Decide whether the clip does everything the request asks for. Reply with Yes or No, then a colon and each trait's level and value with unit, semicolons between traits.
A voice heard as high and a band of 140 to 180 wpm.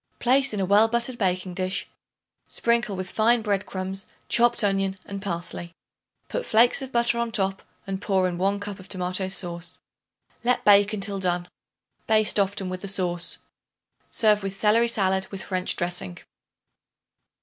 Yes: high, 195 Hz; average, 160 wpm